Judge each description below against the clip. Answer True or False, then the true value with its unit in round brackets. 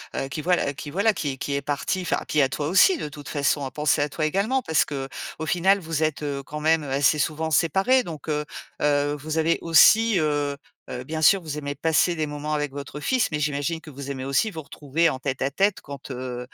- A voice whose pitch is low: False (150 Hz)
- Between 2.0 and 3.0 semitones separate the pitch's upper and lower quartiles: True (2.5 semitones)